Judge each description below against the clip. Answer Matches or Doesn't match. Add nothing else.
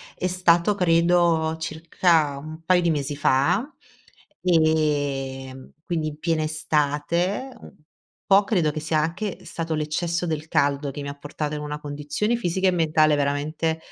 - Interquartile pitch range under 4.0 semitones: Matches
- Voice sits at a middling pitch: Matches